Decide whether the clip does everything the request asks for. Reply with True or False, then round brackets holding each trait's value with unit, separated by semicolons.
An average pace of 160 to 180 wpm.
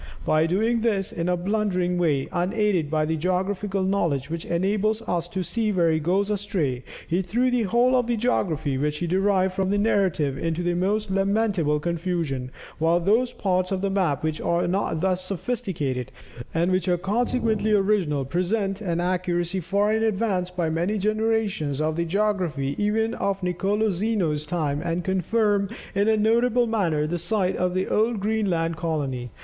True (175 wpm)